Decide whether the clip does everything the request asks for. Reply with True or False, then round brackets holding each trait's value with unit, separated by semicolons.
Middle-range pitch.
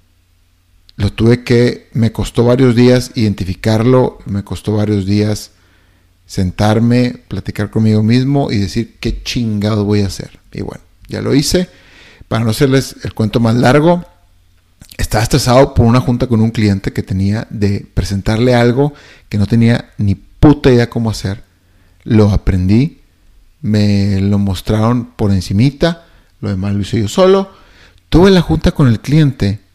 False (110 Hz)